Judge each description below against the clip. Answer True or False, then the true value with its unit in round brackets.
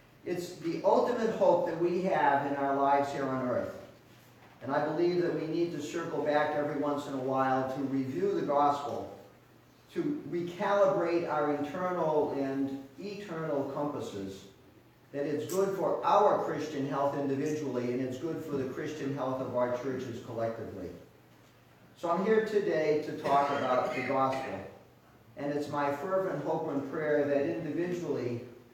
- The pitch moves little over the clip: False (3.9 semitones)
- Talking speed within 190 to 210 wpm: False (155 wpm)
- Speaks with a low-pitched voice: False (145 Hz)